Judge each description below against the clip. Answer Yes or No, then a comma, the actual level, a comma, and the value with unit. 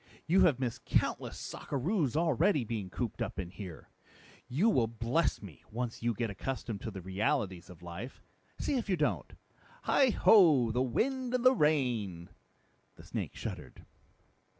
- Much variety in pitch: Yes, wide, 8.4 semitones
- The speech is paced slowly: No, average, 150 wpm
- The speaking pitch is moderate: No, low, 125 Hz